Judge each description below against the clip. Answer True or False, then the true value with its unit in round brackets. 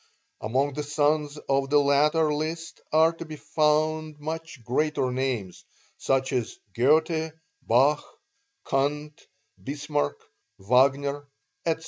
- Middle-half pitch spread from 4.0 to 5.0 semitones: False (2.5 semitones)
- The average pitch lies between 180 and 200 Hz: False (145 Hz)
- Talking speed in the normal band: False (110 wpm)